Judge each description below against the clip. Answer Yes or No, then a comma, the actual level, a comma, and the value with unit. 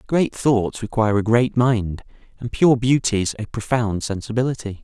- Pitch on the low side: Yes, low, 115 Hz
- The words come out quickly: No, average, 150 wpm